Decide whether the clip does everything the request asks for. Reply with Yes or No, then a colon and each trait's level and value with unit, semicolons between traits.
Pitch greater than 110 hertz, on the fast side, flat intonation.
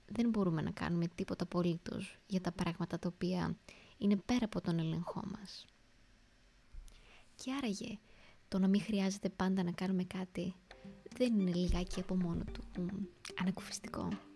No: medium, 185 Hz; average, 140 wpm; narrow, 2.3 semitones